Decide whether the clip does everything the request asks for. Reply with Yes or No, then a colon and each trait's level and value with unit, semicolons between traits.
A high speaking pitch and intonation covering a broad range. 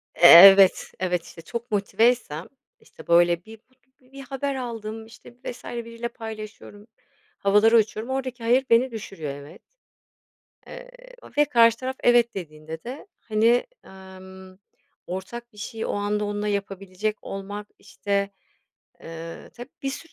No: high, 215 Hz; average, 3.9 semitones